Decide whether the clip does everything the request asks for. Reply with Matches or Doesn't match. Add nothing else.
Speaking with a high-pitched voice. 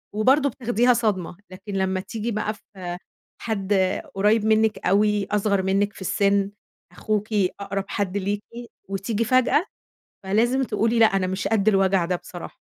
Matches